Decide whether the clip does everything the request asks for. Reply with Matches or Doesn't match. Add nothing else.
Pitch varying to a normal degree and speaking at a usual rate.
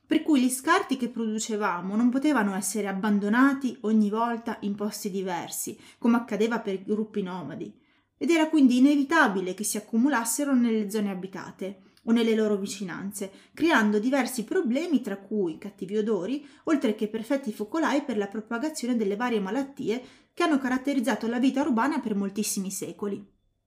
Matches